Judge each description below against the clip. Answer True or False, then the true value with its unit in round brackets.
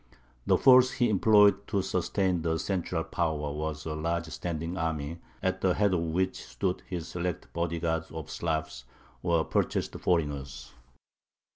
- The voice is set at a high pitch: False (85 Hz)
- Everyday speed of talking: True (150 wpm)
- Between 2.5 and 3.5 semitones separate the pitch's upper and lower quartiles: True (2.9 semitones)